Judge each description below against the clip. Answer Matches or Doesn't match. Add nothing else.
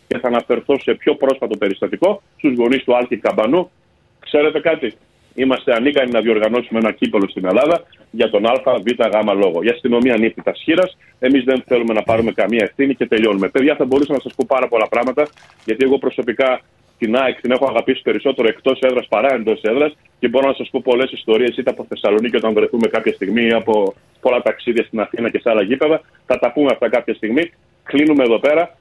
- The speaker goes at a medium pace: Doesn't match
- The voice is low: Matches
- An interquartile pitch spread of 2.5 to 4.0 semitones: Matches